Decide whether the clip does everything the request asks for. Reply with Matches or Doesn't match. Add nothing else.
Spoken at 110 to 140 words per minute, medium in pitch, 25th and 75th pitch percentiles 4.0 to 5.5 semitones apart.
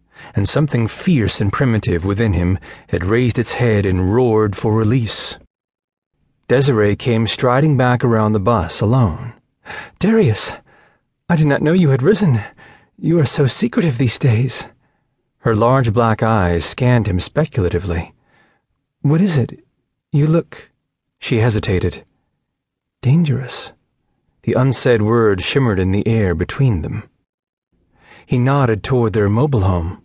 Doesn't match